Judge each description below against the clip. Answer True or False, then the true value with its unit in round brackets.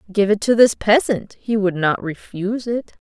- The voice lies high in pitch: True (210 Hz)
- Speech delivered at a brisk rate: False (195 wpm)